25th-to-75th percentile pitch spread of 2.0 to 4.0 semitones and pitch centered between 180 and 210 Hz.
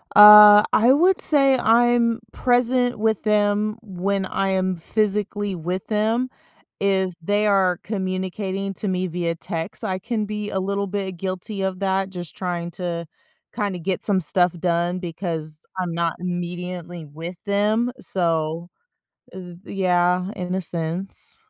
Yes: average, 2.9 semitones; high, 190 Hz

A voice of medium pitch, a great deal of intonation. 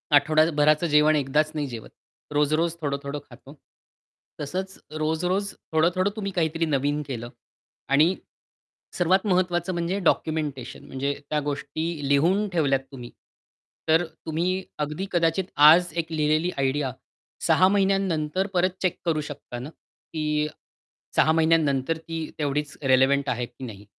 No: medium, 155 Hz; average, 3.3 semitones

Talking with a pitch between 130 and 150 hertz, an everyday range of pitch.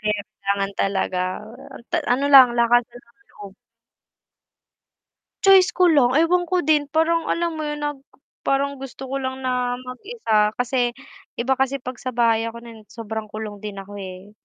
No: very high, 250 Hz; average, 4.6 semitones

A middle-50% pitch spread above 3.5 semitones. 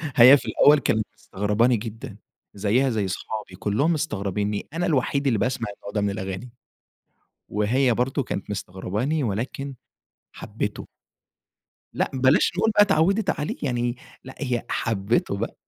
Yes: average, 5.0 semitones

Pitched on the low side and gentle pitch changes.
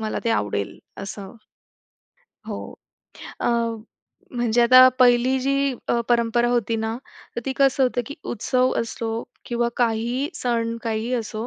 No: high, 235 Hz; narrow, 2.0 semitones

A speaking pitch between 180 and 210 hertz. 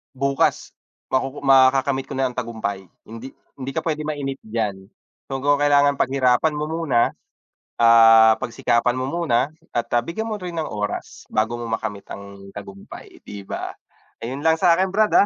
No: low, 130 Hz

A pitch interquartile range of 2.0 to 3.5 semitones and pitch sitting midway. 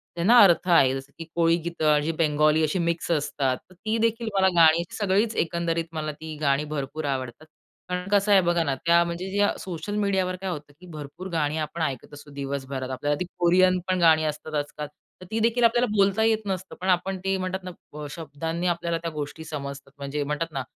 No: average, 4.0 semitones; medium, 165 Hz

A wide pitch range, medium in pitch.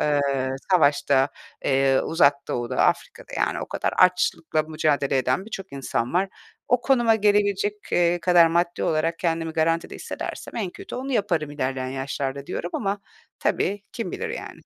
Yes: wide, 5.7 semitones; medium, 165 Hz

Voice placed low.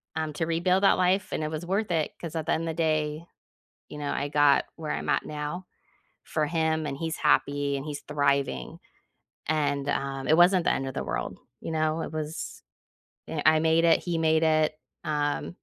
No: medium, 155 Hz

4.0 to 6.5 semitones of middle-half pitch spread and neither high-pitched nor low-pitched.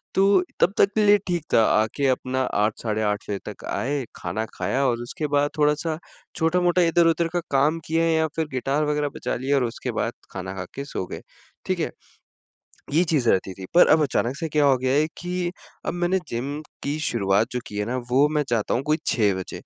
Yes: wide, 5.4 semitones; medium, 145 Hz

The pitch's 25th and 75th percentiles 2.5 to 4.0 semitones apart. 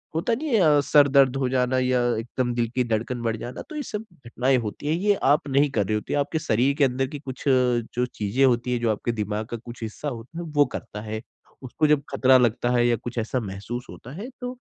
Yes: average, 3.4 semitones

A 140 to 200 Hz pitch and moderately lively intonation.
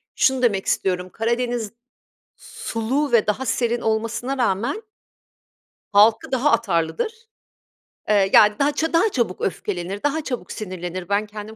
No: high, 220 Hz; average, 4.3 semitones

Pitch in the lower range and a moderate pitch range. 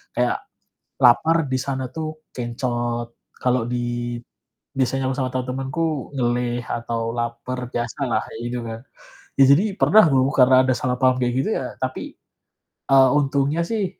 No: low, 130 Hz; narrow, 2.2 semitones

